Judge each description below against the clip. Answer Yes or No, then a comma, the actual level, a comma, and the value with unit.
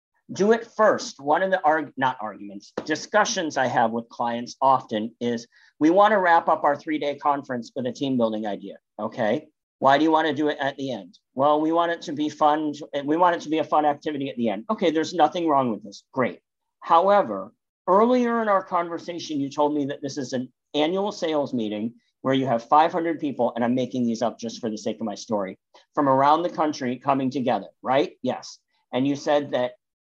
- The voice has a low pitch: No, medium, 145 Hz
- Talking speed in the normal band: No, fast, 220 wpm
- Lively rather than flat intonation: No, average, 4.7 semitones